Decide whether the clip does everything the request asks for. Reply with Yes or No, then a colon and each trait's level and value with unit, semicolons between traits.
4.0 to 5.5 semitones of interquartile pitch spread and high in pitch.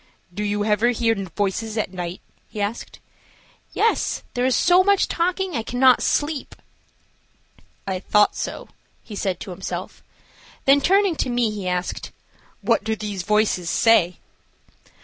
Yes: average, 4.7 semitones; high, 215 Hz